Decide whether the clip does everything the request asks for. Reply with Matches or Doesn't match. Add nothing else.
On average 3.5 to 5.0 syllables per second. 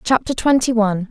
Doesn't match